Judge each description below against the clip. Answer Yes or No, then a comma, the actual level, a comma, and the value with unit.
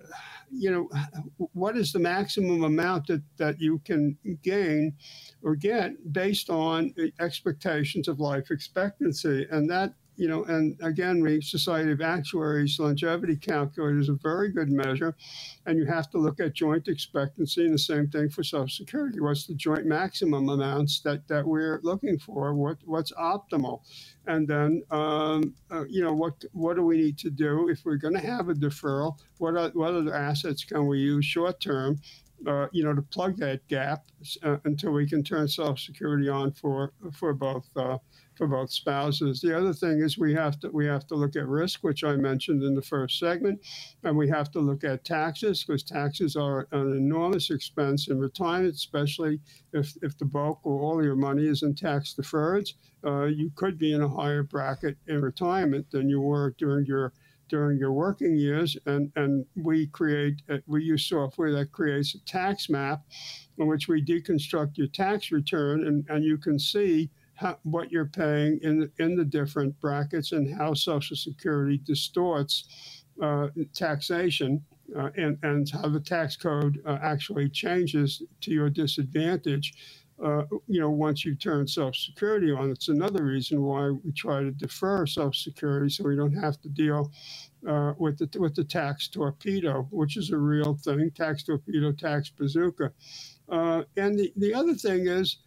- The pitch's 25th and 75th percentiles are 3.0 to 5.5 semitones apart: No, narrow, 2.5 semitones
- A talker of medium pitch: Yes, medium, 150 Hz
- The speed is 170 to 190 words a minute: Yes, average, 180 wpm